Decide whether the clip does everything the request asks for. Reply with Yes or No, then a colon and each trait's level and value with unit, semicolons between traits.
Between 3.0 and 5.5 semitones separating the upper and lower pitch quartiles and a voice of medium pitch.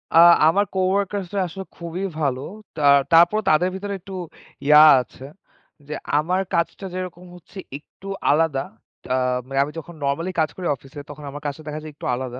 Yes: average, 4.1 semitones; medium, 165 Hz